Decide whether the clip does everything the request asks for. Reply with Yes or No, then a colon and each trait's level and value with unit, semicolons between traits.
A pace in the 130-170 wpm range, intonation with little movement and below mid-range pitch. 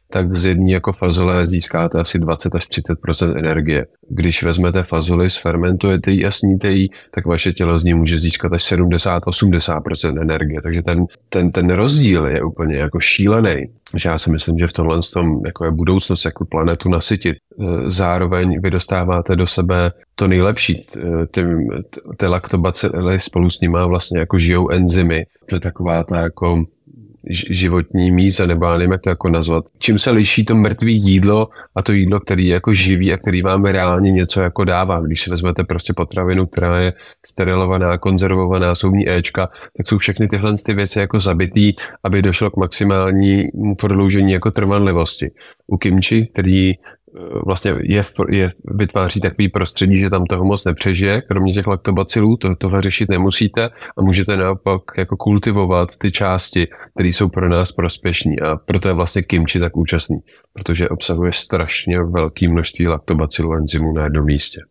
Yes: average, 165 wpm; narrow, 2.2 semitones; very low, 90 Hz